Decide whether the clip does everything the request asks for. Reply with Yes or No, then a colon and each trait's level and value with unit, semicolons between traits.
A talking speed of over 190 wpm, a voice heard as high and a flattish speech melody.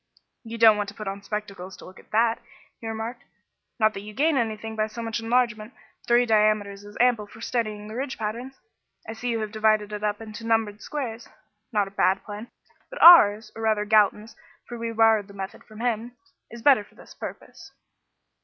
Yes: average, 200 wpm; high, 220 Hz; narrow, 1.8 semitones